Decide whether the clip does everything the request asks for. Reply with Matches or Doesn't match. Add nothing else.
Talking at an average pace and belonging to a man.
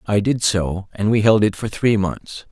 Doesn't match